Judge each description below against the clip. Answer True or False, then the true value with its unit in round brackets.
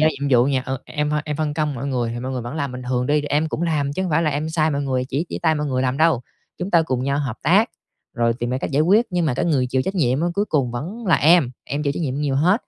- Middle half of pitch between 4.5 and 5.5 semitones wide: False (3.6 semitones)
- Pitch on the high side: False (145 Hz)